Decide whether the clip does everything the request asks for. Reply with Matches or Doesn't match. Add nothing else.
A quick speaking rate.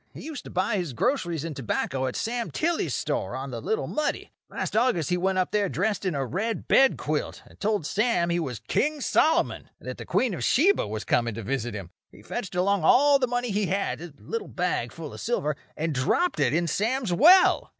Matches